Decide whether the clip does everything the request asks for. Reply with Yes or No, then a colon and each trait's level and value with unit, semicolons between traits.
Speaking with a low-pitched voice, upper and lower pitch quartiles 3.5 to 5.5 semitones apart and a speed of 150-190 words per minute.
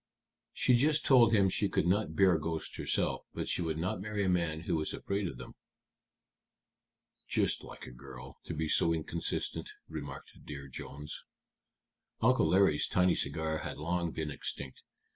Yes: very low, 85 Hz; average, 4.4 semitones; average, 160 wpm